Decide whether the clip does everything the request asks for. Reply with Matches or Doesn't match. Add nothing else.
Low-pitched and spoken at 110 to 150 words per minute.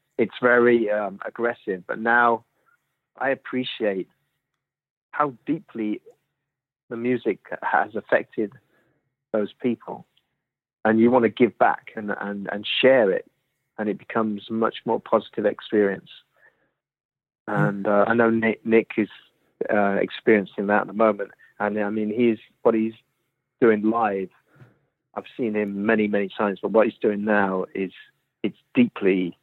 Matches